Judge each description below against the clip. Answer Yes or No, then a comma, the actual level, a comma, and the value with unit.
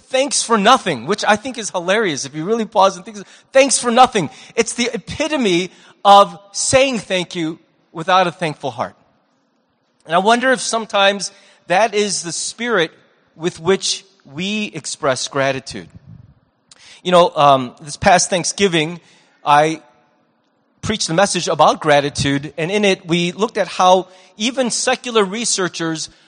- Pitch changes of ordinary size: Yes, average, 4.8 semitones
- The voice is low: No, high, 190 Hz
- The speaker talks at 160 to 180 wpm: No, average, 145 wpm